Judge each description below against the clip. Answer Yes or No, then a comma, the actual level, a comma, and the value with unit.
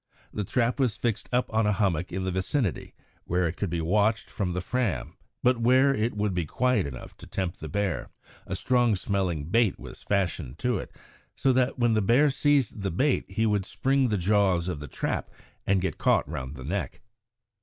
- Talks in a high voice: No, low, 100 Hz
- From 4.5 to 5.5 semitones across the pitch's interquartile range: Yes, average, 5.2 semitones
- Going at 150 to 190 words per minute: No, fast, 205 wpm